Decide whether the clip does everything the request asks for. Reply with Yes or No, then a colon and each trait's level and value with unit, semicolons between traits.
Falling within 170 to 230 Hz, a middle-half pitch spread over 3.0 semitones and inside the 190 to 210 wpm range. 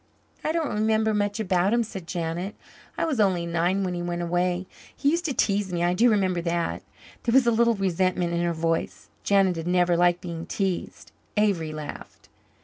Yes: medium, 185 Hz; average, 3.4 semitones; average, 195 wpm